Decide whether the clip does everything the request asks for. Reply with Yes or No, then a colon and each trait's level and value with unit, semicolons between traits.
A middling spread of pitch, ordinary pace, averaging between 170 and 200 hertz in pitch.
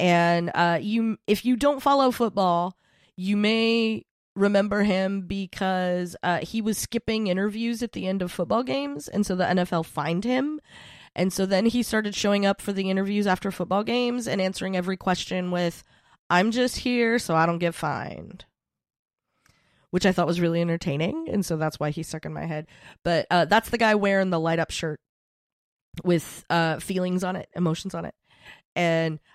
Yes: average, 3.5 semitones; average, 185 wpm; medium, 185 Hz